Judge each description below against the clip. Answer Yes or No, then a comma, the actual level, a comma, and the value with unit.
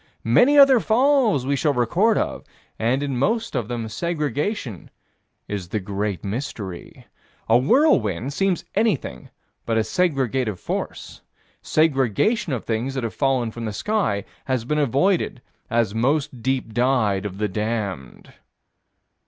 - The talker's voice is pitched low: Yes, low, 125 Hz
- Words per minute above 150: No, average, 140 wpm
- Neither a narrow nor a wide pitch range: No, wide, 6.3 semitones